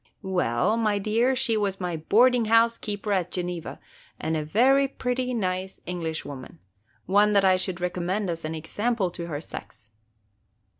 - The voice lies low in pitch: No, high, 190 Hz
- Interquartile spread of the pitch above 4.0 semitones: Yes, average, 4.8 semitones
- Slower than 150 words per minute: No, average, 160 wpm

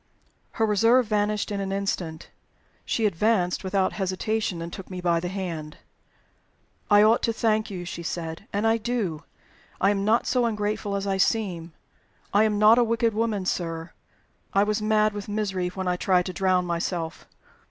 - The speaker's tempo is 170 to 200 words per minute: Yes, average, 175 wpm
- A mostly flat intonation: No, average, 3.2 semitones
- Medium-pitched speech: No, high, 200 Hz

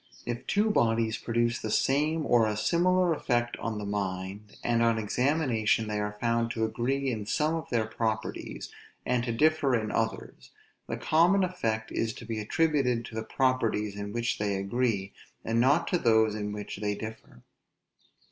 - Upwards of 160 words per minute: Yes, average, 175 wpm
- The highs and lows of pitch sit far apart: No, average, 3.7 semitones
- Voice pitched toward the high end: No, low, 115 Hz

